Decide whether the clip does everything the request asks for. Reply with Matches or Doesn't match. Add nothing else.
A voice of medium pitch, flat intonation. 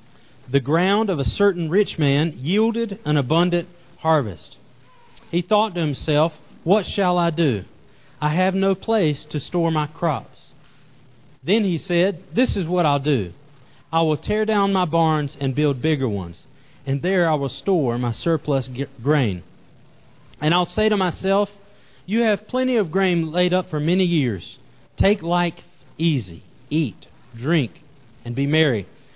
Doesn't match